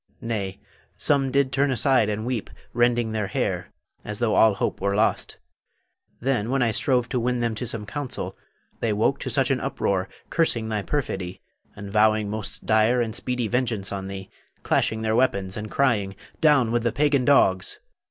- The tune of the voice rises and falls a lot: No, average, 3.4 semitones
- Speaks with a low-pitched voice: Yes, low, 115 Hz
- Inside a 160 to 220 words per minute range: Yes, average, 180 wpm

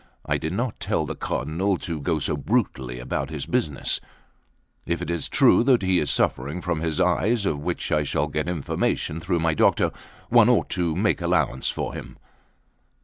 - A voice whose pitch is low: Yes, very low, 80 Hz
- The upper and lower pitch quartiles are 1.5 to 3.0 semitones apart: No, average, 3.6 semitones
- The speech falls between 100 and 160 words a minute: No, average, 185 wpm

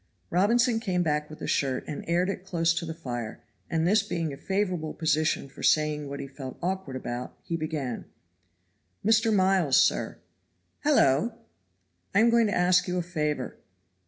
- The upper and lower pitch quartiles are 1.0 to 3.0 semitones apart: No, average, 4.2 semitones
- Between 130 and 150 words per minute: No, average, 170 wpm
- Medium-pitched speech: Yes, medium, 165 Hz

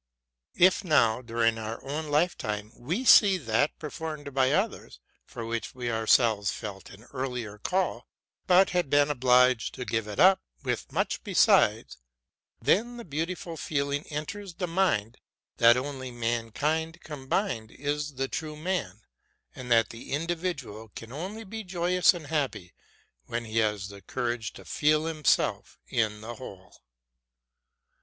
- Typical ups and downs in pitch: No, wide, 6.3 semitones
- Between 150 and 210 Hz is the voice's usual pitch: No, medium, 140 Hz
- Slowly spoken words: No, average, 145 wpm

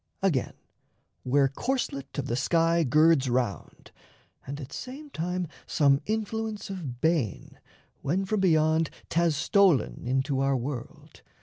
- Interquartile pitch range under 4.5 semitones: No, wide, 5.5 semitones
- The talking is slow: Yes, slow, 125 wpm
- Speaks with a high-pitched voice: No, medium, 155 Hz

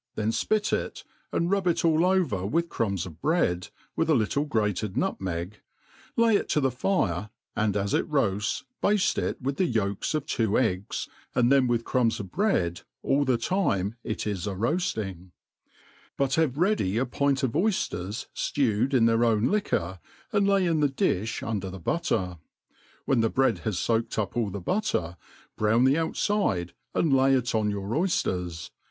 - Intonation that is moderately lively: No, wide, 7.7 semitones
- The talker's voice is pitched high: No, low, 115 Hz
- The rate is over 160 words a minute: Yes, average, 175 wpm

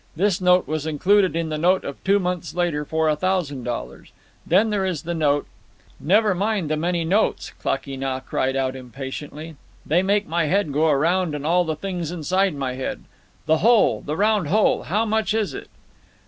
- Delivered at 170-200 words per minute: Yes, average, 190 wpm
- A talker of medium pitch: Yes, medium, 170 Hz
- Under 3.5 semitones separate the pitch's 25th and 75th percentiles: No, average, 4.3 semitones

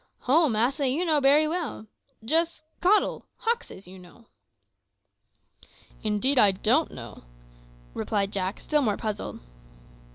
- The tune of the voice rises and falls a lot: Yes, wide, 7.0 semitones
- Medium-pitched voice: No, very high, 260 Hz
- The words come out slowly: Yes, slow, 120 wpm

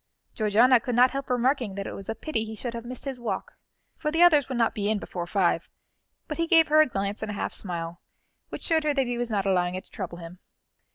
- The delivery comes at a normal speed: No, fast, 260 wpm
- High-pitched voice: Yes, high, 230 Hz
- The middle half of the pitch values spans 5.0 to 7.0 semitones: Yes, wide, 5.4 semitones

